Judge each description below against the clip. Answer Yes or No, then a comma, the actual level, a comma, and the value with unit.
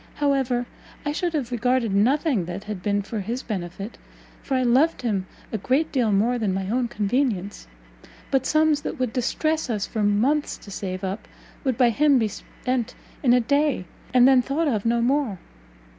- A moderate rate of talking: Yes, average, 190 wpm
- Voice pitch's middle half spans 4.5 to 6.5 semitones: Yes, average, 4.8 semitones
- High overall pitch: Yes, high, 245 Hz